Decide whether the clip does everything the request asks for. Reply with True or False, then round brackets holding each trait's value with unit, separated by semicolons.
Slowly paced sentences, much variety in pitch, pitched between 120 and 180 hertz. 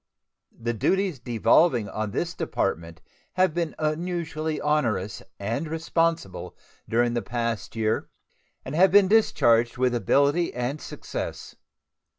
True (120 wpm; 6.2 semitones; 135 Hz)